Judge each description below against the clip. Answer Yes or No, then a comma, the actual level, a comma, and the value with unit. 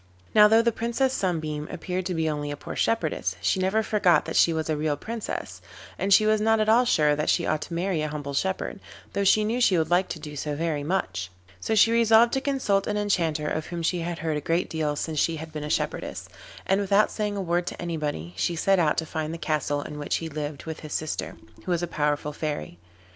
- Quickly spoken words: Yes, fast, 245 wpm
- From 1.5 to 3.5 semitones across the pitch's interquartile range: No, average, 4.9 semitones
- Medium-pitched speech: Yes, medium, 165 Hz